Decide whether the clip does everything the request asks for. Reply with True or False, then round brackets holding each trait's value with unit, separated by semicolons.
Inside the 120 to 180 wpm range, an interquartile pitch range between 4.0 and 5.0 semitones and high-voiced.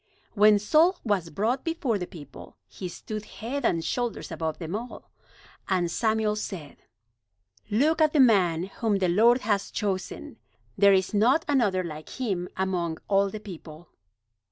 True (155 wpm; 4.5 semitones; 205 Hz)